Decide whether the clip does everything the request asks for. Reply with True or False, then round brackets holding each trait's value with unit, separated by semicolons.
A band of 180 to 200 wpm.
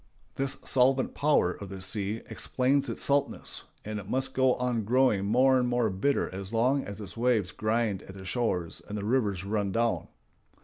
True (185 wpm)